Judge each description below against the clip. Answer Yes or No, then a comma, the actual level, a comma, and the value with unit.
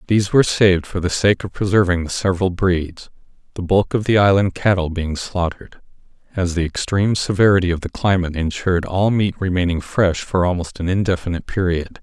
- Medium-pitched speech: No, very low, 95 Hz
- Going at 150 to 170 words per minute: No, average, 180 wpm